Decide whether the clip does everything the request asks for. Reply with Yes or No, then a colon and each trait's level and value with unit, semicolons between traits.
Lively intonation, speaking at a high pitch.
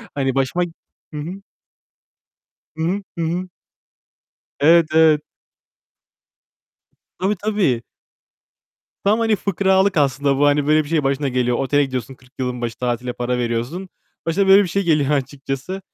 No: wide, 5.7 semitones; medium, 150 Hz